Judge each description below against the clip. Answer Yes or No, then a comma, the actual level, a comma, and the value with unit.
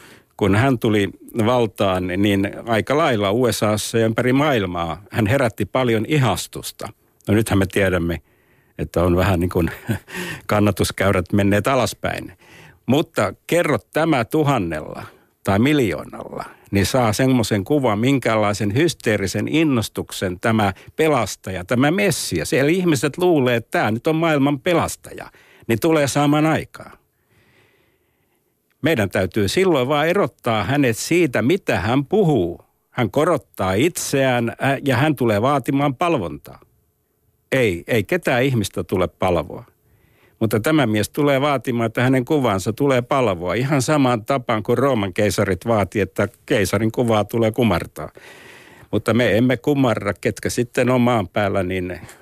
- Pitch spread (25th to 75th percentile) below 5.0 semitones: No, average, 5.3 semitones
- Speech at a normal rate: Yes, average, 130 wpm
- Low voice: Yes, low, 115 Hz